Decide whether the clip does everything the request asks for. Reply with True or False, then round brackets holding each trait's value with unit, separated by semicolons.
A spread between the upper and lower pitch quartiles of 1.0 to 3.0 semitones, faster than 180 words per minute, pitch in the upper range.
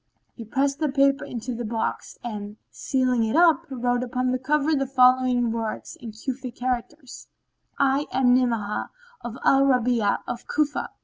False (2.5 semitones; 160 wpm; 250 Hz)